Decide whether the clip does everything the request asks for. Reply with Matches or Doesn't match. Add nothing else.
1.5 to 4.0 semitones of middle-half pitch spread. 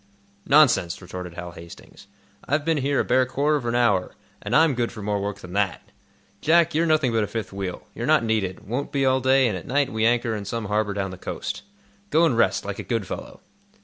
Doesn't match